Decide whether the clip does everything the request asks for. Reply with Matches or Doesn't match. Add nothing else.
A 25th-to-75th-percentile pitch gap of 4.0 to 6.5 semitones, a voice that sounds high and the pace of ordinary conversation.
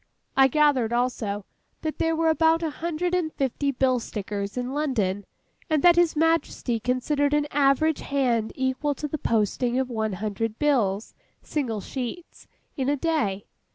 Matches